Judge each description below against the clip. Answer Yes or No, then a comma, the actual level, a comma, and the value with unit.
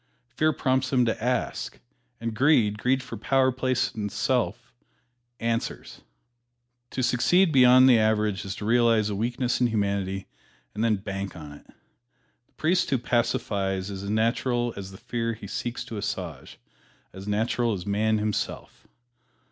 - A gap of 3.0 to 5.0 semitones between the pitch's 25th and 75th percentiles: Yes, average, 3.4 semitones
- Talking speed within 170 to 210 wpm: No, average, 155 wpm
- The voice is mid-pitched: No, low, 115 Hz